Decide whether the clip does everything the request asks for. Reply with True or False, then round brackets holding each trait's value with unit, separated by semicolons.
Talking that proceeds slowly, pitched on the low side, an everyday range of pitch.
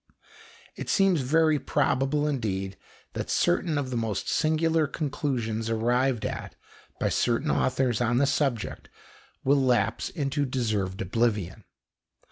True (120 wpm; 130 Hz; 4.5 semitones)